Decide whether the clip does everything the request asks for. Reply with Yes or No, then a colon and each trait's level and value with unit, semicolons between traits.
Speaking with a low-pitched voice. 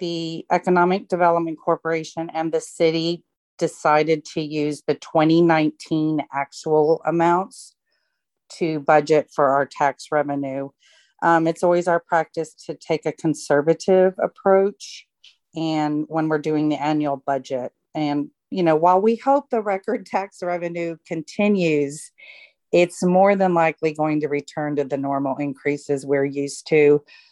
No: medium, 160 Hz